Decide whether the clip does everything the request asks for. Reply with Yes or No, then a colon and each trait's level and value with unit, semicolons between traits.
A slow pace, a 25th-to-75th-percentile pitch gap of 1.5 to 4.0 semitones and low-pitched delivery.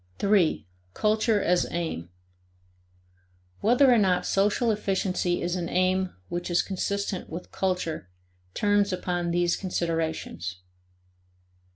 No: slow, 105 wpm; average, 2.7 semitones; medium, 185 Hz